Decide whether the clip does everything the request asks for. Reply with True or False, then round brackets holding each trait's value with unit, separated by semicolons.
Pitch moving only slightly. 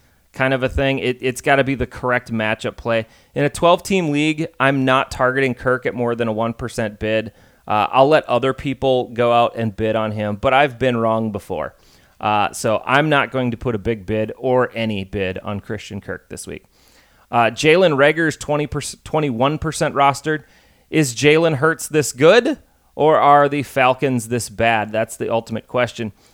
False (4.0 semitones)